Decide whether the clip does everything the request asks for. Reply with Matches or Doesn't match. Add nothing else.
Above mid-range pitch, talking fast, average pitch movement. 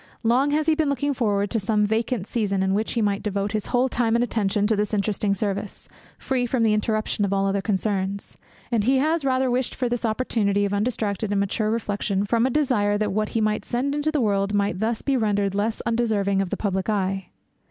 Matches